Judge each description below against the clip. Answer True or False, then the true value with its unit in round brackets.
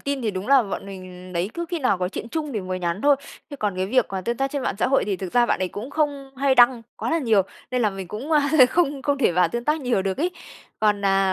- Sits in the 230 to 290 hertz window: True (235 Hz)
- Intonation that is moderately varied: False (6.4 semitones)